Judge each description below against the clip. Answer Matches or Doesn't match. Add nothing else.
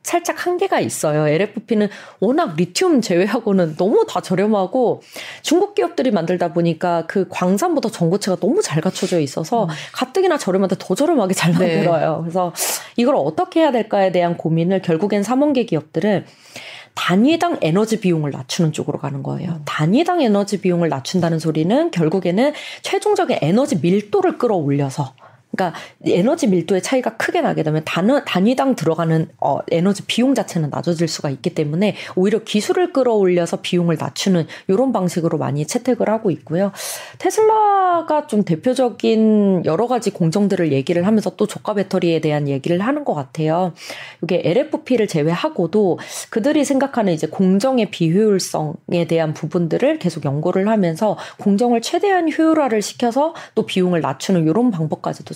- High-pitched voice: Matches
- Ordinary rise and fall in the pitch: Doesn't match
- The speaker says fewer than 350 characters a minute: Doesn't match